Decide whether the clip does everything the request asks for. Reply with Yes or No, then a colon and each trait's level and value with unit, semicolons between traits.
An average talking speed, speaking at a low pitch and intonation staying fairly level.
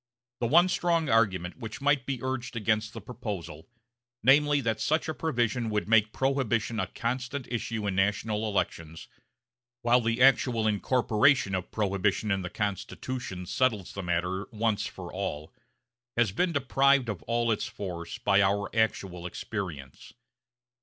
No: average, 145 wpm; low, 110 Hz; average, 4.4 semitones